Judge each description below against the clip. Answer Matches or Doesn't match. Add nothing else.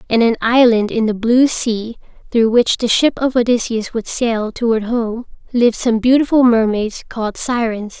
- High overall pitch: Matches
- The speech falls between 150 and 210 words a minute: Matches